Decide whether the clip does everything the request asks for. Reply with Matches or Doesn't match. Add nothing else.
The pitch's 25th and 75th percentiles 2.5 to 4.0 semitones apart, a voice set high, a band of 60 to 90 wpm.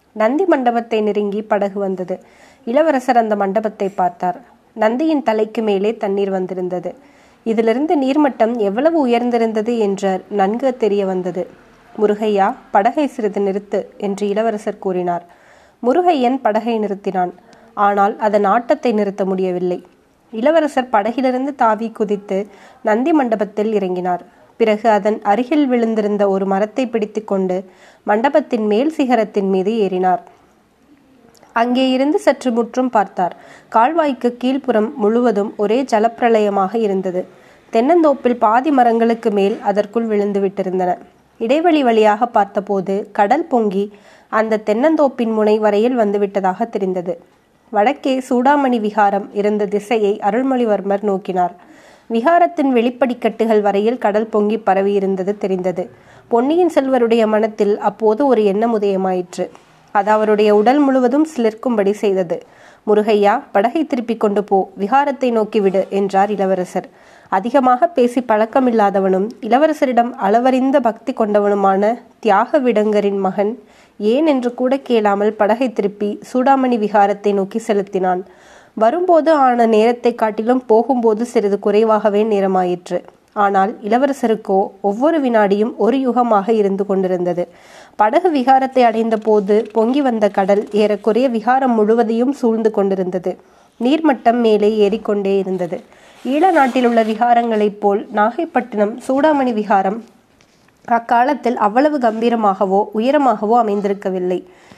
Doesn't match